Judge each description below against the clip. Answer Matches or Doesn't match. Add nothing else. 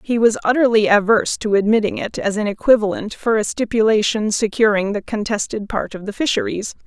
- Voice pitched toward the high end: Matches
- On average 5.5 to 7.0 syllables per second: Matches